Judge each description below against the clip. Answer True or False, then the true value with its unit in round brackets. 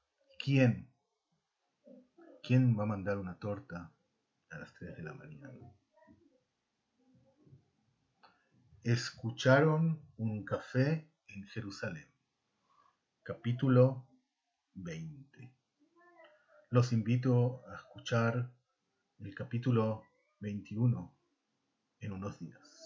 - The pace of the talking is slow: True (80 wpm)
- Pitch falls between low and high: False (125 Hz)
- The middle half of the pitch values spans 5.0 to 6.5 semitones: True (5.5 semitones)